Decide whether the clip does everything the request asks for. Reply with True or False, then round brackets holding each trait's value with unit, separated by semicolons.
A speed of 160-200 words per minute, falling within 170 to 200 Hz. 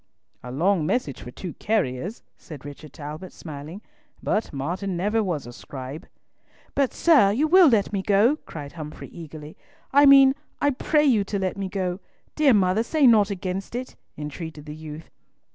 True (170 wpm; 190 Hz)